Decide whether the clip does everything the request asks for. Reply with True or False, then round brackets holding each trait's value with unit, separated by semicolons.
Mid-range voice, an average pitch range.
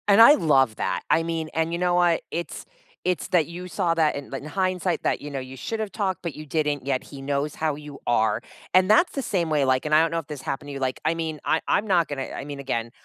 True (160 Hz; 4.1 semitones)